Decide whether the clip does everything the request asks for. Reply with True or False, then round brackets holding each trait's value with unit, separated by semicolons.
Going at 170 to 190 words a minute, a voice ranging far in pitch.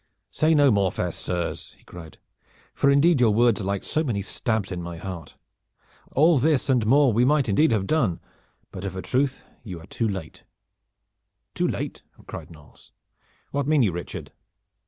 True (175 wpm; 7.1 semitones)